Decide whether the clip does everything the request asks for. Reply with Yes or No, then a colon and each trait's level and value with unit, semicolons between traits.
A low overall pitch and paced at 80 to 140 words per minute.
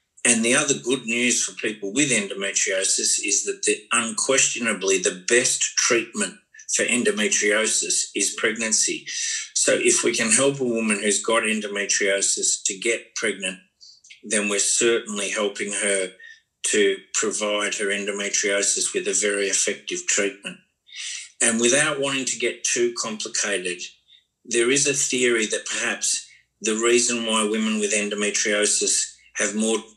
Yes: low, 115 Hz; slow, 135 wpm